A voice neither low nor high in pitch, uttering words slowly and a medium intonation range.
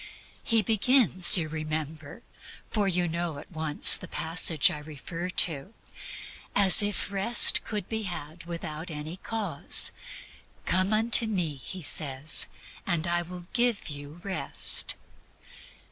Yes: medium, 175 Hz; slow, 130 wpm; average, 4.4 semitones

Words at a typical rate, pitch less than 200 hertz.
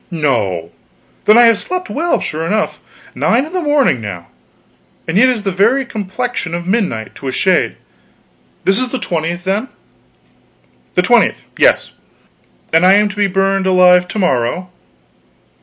Yes: average, 160 wpm; high, 190 Hz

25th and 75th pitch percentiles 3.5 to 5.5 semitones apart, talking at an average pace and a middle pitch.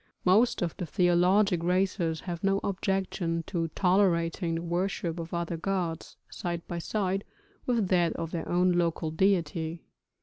No: narrow, 2.4 semitones; average, 145 wpm; medium, 175 Hz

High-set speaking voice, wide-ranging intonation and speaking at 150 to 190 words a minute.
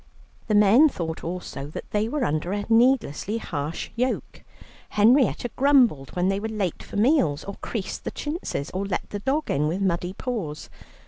Yes: high, 205 Hz; wide, 6.2 semitones; average, 175 wpm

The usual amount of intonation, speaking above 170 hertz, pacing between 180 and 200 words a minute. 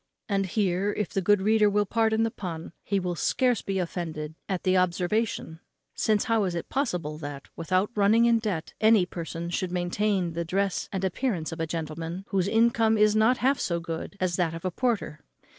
Yes: average, 4.1 semitones; high, 190 Hz; average, 195 wpm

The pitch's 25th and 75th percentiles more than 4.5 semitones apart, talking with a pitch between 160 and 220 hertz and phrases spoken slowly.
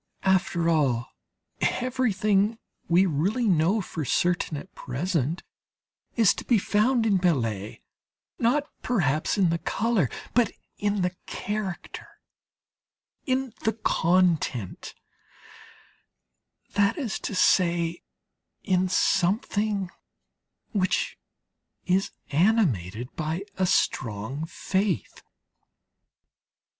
Yes: average, 4.9 semitones; medium, 185 Hz; slow, 90 wpm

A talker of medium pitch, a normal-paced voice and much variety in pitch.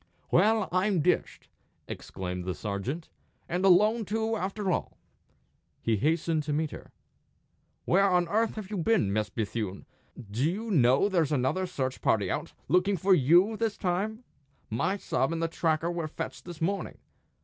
Yes: medium, 175 Hz; average, 160 wpm; wide, 6.9 semitones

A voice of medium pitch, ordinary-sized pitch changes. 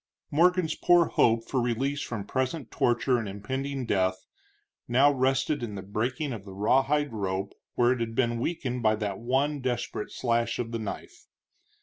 No: low, 120 Hz; average, 3.7 semitones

